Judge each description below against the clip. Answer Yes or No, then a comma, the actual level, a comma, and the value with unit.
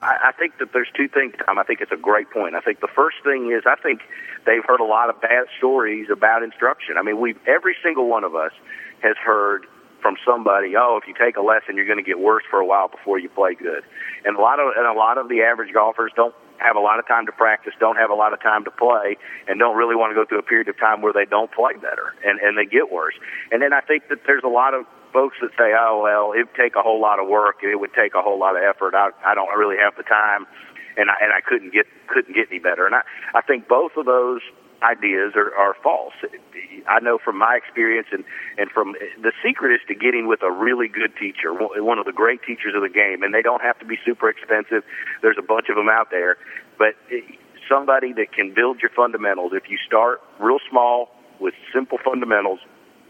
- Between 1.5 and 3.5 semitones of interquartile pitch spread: No, average, 4.6 semitones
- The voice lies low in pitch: Yes, low, 120 Hz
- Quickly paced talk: Yes, fast, 250 wpm